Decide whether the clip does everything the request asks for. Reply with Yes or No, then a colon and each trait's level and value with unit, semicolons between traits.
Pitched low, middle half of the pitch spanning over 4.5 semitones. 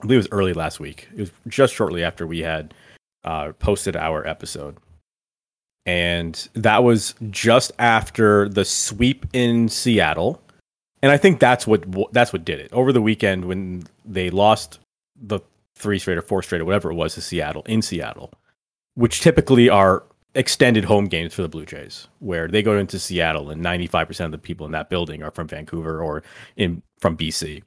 Yes: very low, 95 Hz; average, 4.9 semitones